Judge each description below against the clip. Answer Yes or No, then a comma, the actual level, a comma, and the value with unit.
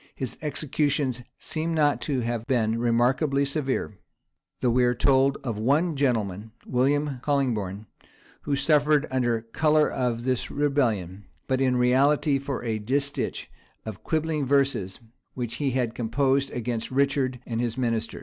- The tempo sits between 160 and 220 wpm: No, average, 140 wpm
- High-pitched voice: No, low, 130 Hz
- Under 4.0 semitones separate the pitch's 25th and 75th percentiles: Yes, average, 3.4 semitones